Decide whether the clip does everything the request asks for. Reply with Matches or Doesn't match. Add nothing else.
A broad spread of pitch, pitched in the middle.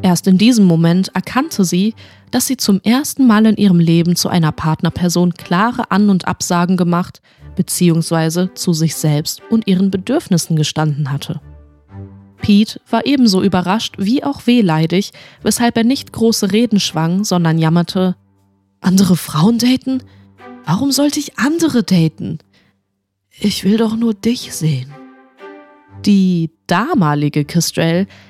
Matches